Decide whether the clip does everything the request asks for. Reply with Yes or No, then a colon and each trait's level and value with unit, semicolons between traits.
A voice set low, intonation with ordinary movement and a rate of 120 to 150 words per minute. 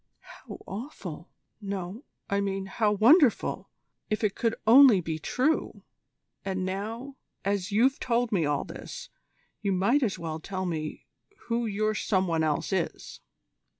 No: high, 200 Hz; average, 3.8 semitones; average, 145 wpm